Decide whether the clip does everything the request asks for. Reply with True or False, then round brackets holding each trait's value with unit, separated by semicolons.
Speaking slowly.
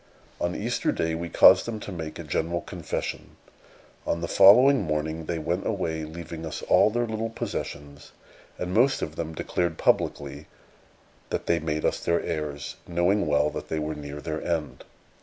False (175 wpm)